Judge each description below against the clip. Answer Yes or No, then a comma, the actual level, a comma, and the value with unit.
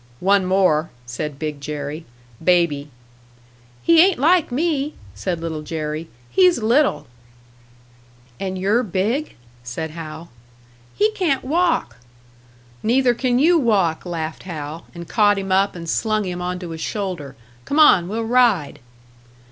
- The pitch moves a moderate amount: No, wide, 7.5 semitones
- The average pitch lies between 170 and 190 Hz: Yes, medium, 185 Hz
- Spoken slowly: Yes, slow, 130 wpm